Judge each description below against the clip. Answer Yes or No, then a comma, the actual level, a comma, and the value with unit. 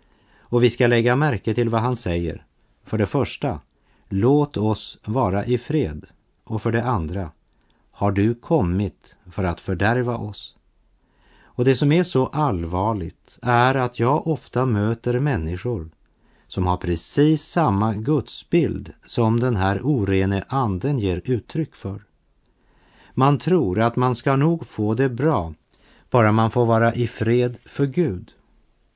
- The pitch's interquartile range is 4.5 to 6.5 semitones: Yes, average, 4.9 semitones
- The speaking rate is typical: Yes, average, 145 wpm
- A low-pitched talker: Yes, low, 115 Hz